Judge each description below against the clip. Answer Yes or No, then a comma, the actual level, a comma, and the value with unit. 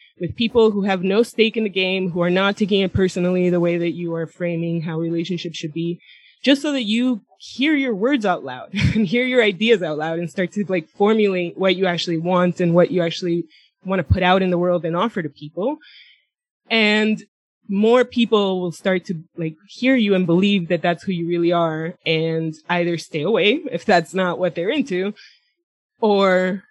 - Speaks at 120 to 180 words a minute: No, fast, 205 wpm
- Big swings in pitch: No, average, 3.8 semitones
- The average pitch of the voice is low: No, medium, 185 Hz